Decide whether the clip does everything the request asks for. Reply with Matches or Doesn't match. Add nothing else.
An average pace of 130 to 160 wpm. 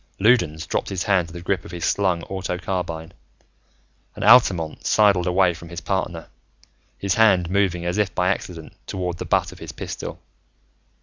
Doesn't match